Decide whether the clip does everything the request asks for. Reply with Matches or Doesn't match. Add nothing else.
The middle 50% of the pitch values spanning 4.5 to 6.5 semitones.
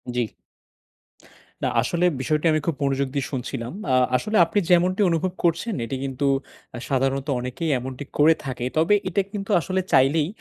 Matches